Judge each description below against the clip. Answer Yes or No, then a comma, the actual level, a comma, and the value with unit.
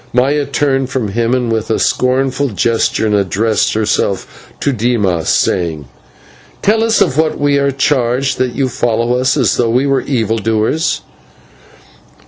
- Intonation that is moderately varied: Yes, average, 3.7 semitones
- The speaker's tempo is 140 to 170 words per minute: Yes, average, 150 wpm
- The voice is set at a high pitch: No, low, 125 Hz